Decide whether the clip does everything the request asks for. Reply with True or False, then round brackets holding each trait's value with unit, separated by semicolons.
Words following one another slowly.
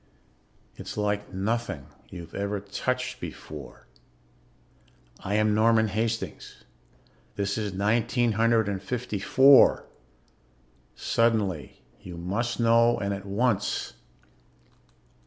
True (100 wpm)